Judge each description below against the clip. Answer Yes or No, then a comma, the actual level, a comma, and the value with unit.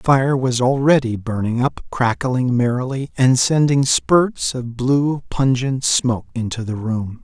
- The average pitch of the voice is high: No, low, 125 Hz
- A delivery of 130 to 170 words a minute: Yes, average, 150 wpm